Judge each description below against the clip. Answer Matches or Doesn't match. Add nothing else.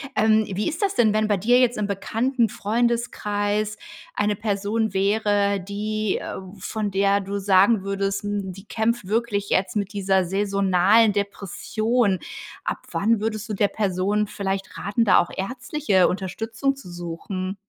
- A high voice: Matches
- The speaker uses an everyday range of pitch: Doesn't match